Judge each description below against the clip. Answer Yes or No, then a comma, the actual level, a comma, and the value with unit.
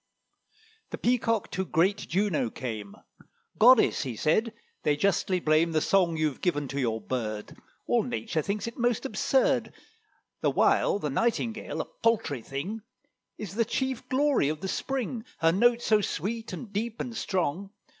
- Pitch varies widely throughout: Yes, wide, 7.1 semitones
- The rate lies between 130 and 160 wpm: Yes, average, 155 wpm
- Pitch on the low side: No, high, 195 Hz